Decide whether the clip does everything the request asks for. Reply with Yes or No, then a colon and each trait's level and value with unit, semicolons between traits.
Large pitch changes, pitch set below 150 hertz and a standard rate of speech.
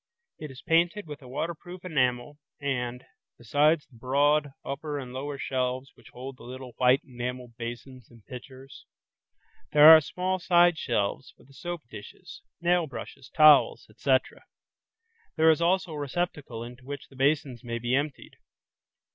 No: average, 3.6 semitones; low, 135 Hz; average, 155 wpm